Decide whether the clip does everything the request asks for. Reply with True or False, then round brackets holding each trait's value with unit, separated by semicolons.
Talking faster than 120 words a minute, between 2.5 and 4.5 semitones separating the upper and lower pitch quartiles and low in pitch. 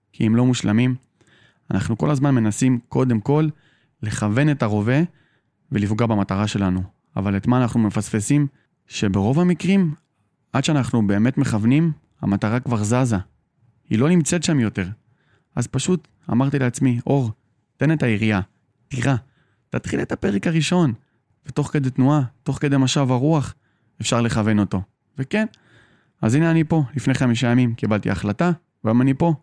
False (145 wpm; 5.1 semitones; 125 Hz)